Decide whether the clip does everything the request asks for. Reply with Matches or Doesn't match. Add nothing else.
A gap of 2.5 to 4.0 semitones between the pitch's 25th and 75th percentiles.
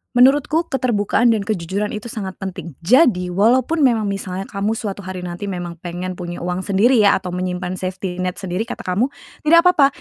Doesn't match